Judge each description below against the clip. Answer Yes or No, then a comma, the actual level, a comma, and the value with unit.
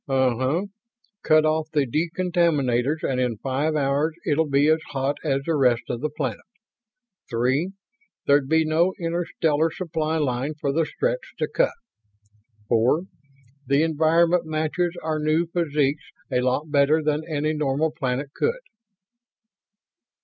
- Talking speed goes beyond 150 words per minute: No, average, 140 wpm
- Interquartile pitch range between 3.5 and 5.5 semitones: No, average, 2.9 semitones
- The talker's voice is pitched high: No, medium, 155 Hz